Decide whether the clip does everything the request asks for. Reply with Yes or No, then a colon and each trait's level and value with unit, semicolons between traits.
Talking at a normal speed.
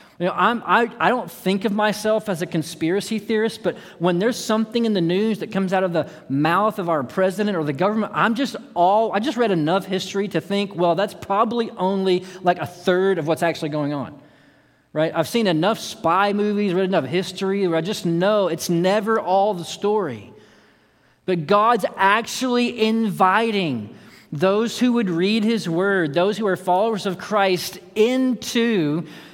Yes: average, 180 wpm